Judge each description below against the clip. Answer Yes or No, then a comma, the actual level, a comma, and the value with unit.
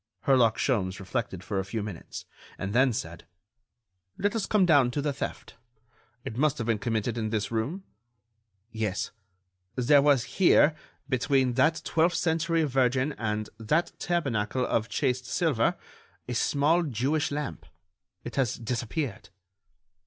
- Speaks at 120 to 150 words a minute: Yes, average, 140 wpm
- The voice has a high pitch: No, low, 130 Hz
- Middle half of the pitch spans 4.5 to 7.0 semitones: Yes, average, 5.1 semitones